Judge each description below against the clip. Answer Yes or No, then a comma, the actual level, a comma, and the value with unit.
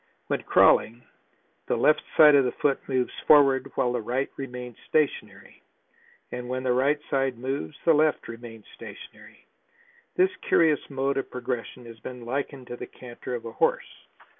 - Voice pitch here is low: Yes, low, 130 Hz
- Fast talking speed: No, average, 165 wpm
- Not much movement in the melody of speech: Yes, narrow, 2.3 semitones